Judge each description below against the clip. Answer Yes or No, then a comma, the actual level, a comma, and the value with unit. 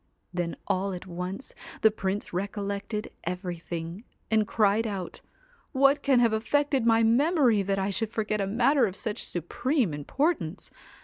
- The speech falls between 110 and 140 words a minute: No, average, 150 wpm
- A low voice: No, high, 210 Hz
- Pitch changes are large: No, average, 4.2 semitones